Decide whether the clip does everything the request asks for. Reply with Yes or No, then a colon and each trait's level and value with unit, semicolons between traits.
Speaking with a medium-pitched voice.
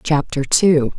Yes: medium, 150 Hz